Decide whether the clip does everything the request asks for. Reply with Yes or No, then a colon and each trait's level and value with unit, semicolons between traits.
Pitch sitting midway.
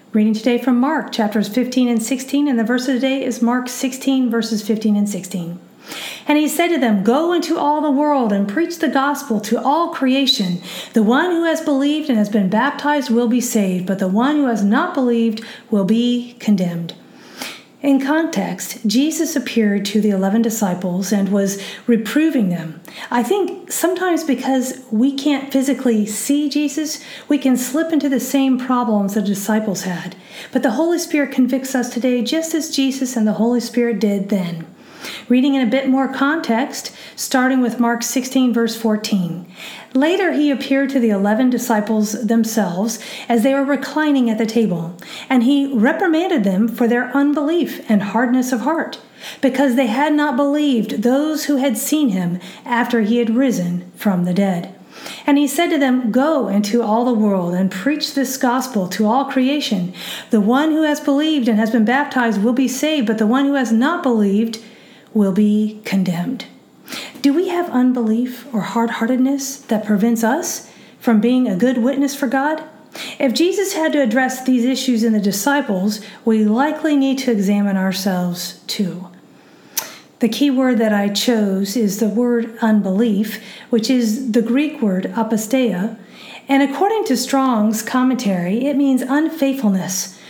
No: high, 245 Hz